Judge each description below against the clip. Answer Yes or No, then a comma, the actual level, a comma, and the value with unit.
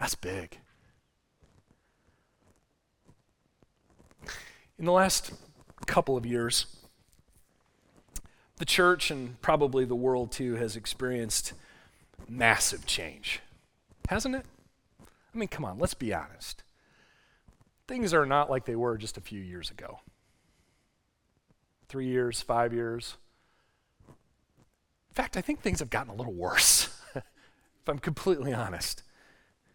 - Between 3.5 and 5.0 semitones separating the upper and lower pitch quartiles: Yes, average, 4.5 semitones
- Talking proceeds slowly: Yes, slow, 115 wpm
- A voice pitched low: Yes, low, 125 Hz